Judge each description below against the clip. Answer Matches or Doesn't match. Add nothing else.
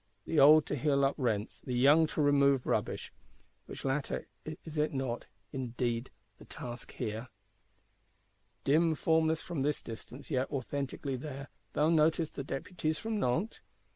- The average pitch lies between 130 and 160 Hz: Matches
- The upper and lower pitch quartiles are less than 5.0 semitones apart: Matches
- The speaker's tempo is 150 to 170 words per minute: Doesn't match